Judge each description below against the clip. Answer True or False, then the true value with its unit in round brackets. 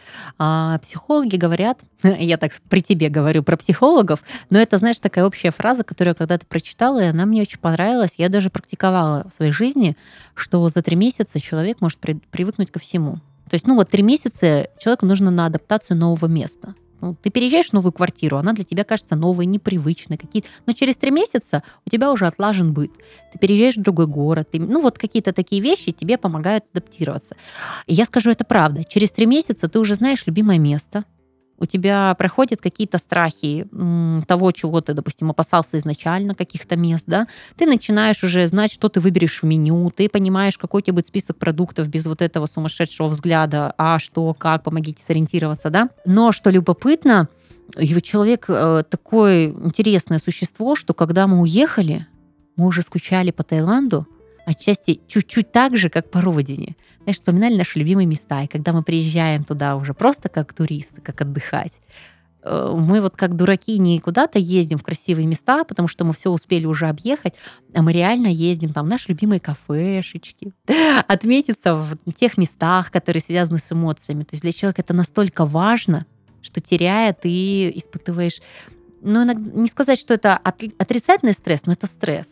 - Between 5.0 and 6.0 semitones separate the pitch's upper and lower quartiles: False (4.3 semitones)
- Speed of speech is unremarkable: False (170 wpm)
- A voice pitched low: False (180 Hz)